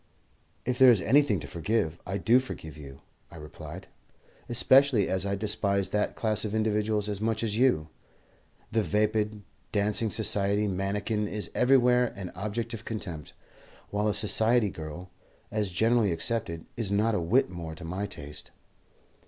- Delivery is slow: No, average, 155 wpm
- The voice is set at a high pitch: No, low, 105 Hz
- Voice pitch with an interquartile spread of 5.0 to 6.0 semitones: No, average, 3.1 semitones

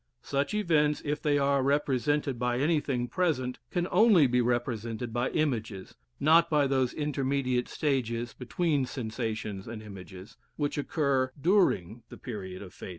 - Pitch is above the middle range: No, low, 130 Hz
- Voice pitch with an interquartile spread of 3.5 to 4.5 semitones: Yes, average, 4.0 semitones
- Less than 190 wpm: Yes, average, 145 wpm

